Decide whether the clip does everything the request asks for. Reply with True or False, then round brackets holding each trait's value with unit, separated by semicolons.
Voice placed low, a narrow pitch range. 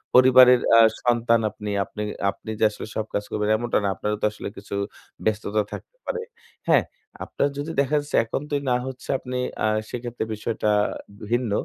False (120 Hz; 3.1 semitones)